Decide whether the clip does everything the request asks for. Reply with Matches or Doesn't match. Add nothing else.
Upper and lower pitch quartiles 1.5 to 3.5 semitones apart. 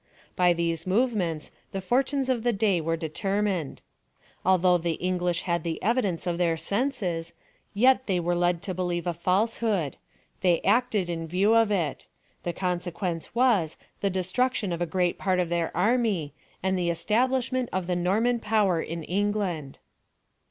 Doesn't match